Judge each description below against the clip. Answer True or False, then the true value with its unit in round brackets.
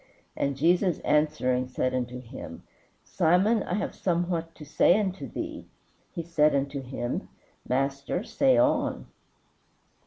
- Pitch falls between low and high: True (155 Hz)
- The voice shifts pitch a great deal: False (4.8 semitones)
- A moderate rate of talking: False (125 wpm)